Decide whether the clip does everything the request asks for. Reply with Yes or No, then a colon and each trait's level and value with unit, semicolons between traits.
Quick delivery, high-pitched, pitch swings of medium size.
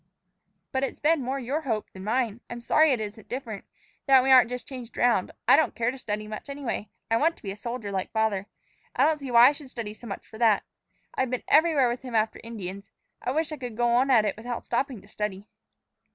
Yes: fast, 240 wpm; high, 240 Hz; average, 3.6 semitones